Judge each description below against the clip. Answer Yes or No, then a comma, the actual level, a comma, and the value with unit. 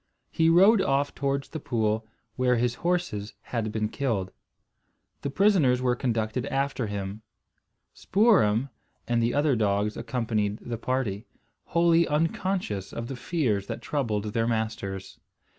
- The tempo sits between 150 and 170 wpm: No, slow, 135 wpm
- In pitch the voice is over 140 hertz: No, low, 120 Hz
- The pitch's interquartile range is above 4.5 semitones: Yes, average, 5.0 semitones